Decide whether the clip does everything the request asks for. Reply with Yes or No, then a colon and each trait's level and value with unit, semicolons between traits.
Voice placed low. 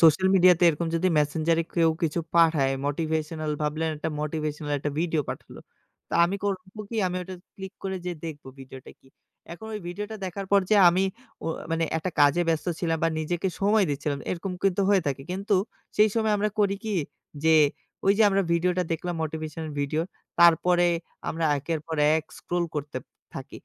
No: medium, 165 Hz